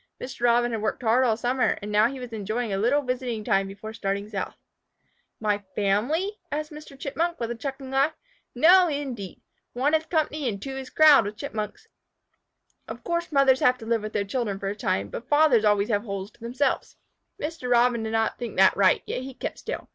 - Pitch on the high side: Yes, high, 240 Hz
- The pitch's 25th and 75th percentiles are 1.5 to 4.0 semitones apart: No, average, 4.7 semitones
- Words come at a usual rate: No, fast, 210 wpm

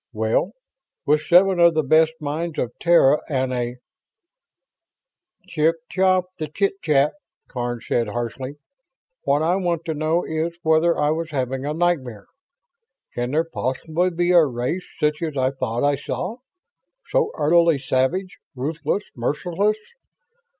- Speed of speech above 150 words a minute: No, average, 145 wpm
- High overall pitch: No, medium, 155 Hz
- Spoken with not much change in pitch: No, average, 4.6 semitones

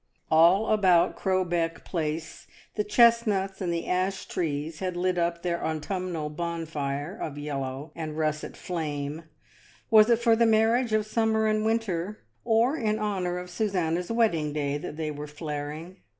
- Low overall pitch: No, medium, 175 Hz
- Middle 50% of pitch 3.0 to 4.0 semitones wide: No, wide, 5.4 semitones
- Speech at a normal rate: Yes, average, 160 wpm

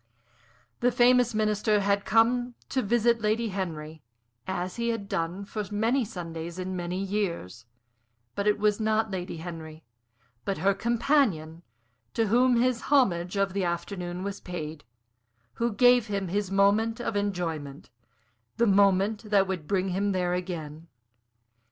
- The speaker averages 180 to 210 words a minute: No, average, 145 wpm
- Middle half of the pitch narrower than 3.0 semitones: No, average, 4.1 semitones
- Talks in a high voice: Yes, high, 200 Hz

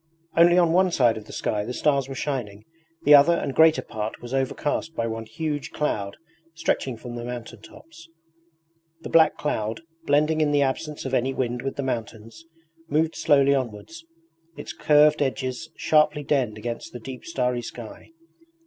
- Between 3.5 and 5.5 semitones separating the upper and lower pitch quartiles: Yes, average, 4.3 semitones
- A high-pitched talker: No, low, 135 Hz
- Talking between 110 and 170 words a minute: Yes, average, 165 wpm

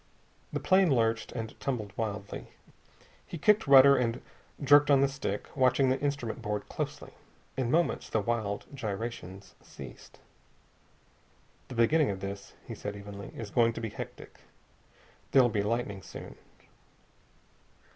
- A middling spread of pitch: Yes, average, 5.0 semitones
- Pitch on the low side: Yes, low, 115 Hz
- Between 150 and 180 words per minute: No, slow, 135 wpm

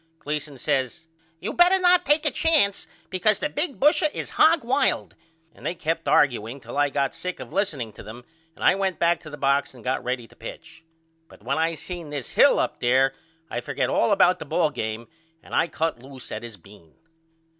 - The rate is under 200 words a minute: No, fast, 205 wpm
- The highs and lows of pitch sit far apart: Yes, wide, 7.4 semitones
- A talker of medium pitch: Yes, medium, 155 Hz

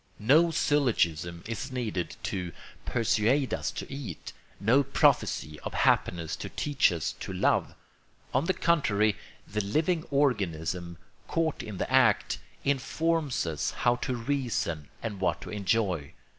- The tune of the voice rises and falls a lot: Yes, wide, 7.7 semitones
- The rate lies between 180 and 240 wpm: No, slow, 135 wpm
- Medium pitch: No, low, 115 Hz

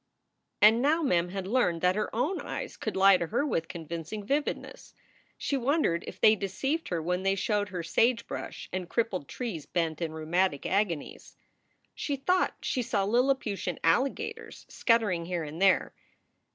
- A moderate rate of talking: Yes, average, 165 wpm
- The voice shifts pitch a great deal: Yes, wide, 6.4 semitones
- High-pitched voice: Yes, high, 195 Hz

